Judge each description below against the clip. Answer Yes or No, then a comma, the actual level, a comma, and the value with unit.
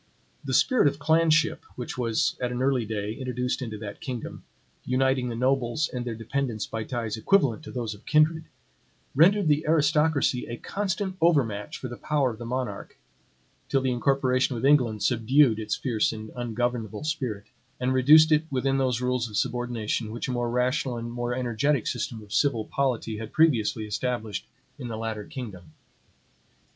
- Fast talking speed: No, average, 170 wpm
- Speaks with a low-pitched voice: Yes, low, 125 Hz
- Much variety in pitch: No, average, 3.6 semitones